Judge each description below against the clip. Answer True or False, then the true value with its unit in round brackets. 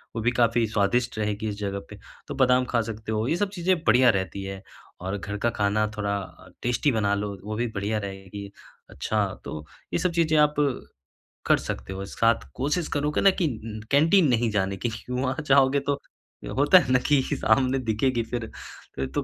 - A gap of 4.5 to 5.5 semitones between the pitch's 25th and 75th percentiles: True (4.9 semitones)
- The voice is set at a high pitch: False (115 Hz)